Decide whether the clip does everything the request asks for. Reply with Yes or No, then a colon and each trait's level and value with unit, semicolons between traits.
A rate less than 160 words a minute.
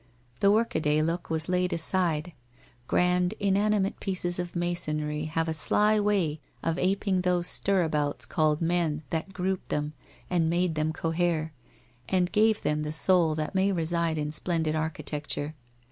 Yes: average, 150 wpm